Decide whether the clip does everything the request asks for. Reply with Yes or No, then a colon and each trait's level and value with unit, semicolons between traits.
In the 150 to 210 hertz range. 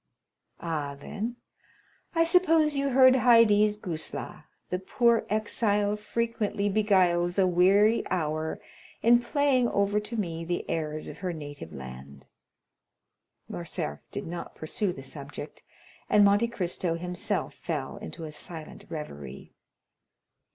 Yes: high, 190 Hz